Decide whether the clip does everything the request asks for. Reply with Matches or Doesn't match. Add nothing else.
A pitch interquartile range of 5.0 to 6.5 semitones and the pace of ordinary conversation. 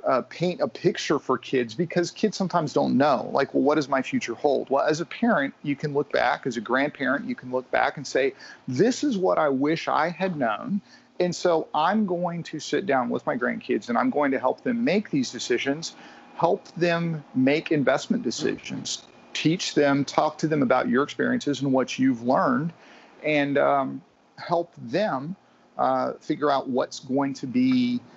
Matches